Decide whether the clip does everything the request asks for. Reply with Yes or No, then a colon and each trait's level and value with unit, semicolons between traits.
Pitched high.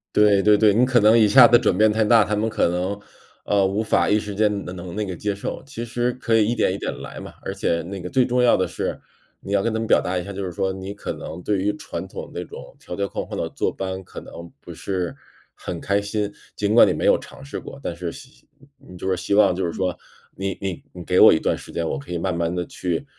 No: low, 100 Hz